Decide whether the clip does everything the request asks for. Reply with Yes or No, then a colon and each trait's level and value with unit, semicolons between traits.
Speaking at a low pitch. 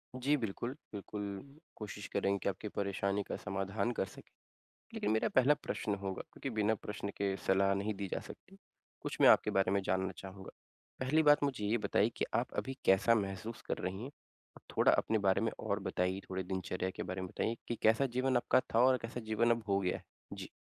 Yes: low, 105 Hz